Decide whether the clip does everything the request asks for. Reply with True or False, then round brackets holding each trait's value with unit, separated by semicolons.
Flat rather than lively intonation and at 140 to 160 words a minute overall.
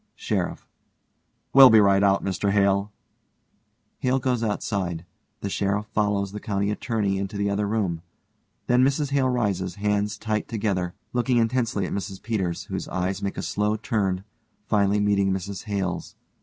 True (2.2 semitones; 155 wpm)